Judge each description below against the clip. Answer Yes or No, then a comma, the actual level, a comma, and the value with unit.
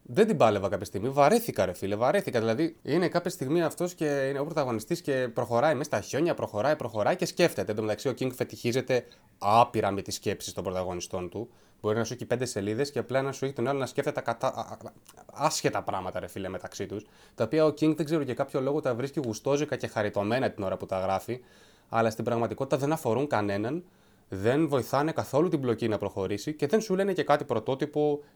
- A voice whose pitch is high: No, low, 130 Hz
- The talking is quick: Yes, fast, 215 wpm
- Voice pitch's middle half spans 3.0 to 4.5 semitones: No, average, 5.2 semitones